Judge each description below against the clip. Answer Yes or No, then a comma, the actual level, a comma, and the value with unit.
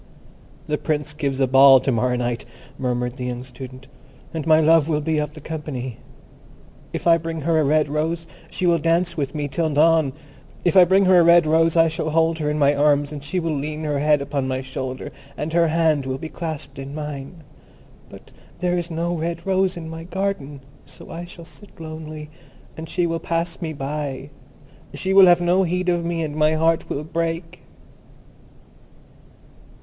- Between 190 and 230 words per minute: Yes, average, 195 wpm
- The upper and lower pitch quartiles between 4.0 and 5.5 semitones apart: No, average, 2.8 semitones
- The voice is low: No, medium, 155 Hz